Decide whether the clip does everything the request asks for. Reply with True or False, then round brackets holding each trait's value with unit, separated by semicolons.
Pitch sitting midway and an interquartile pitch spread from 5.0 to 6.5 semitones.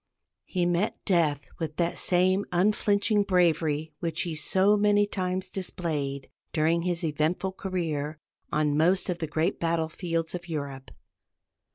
False (170 Hz; 3.1 semitones)